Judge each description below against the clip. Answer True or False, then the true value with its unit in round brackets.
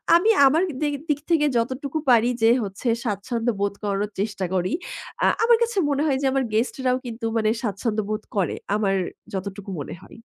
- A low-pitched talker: False (225 Hz)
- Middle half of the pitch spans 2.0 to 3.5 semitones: False (4.9 semitones)